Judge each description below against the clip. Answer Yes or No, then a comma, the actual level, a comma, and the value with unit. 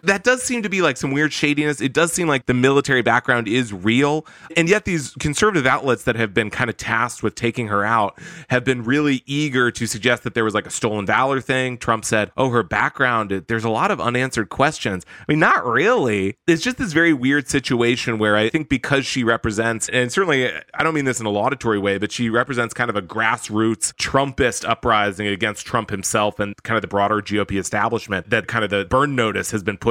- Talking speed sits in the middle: No, fast, 225 wpm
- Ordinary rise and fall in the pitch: Yes, average, 4.2 semitones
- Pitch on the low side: Yes, low, 120 Hz